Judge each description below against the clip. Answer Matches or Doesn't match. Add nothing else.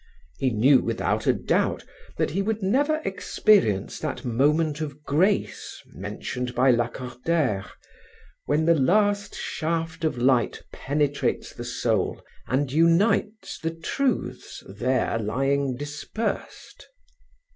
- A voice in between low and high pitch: Matches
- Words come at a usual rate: Doesn't match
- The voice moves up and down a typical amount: Doesn't match